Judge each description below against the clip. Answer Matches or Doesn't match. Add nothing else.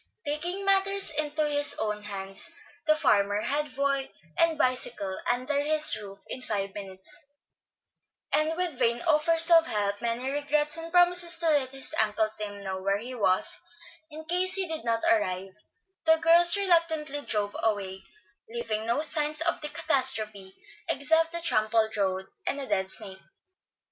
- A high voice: Matches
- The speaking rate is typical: Matches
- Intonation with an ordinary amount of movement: Doesn't match